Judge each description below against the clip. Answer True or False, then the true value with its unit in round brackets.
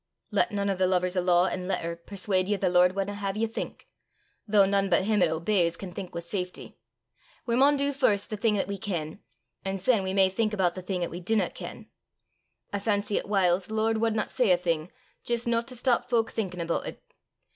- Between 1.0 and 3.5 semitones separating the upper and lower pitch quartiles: True (3.1 semitones)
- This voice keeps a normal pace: False (225 wpm)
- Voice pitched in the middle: False (195 Hz)